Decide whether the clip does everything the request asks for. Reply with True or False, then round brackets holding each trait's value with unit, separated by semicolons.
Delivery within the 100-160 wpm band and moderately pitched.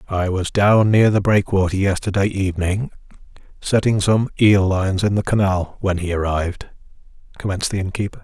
False (155 wpm; 100 Hz)